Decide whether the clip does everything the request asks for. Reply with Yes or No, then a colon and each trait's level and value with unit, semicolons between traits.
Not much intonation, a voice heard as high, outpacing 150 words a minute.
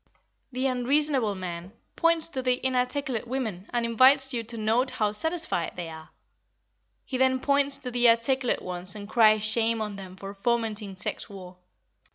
No: average, 4.3 semitones; high, 235 Hz; average, 165 wpm